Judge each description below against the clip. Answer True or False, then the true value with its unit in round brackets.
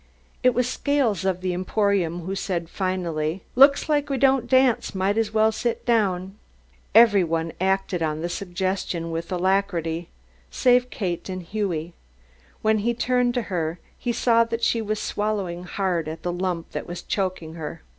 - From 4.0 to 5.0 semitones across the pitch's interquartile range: True (4.7 semitones)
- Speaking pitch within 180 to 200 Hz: True (190 Hz)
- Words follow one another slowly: False (165 wpm)